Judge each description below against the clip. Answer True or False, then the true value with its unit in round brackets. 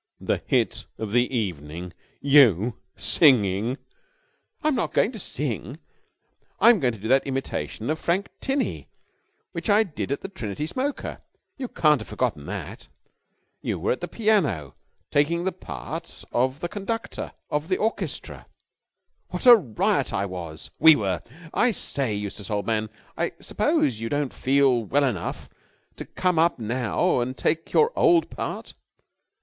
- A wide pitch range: True (8.8 semitones)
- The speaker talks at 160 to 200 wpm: False (150 wpm)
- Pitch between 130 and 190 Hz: True (135 Hz)